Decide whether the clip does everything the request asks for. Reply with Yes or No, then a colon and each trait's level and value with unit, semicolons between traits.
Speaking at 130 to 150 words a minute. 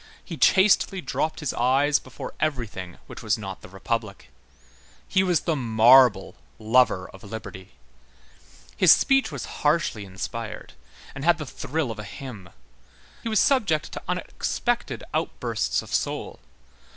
Yes: average, 140 wpm